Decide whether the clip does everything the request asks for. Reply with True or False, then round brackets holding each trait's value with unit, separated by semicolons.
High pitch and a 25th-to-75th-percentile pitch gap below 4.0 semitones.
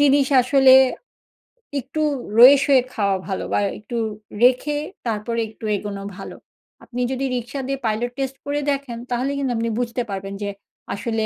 True (245 Hz; 3.6 semitones)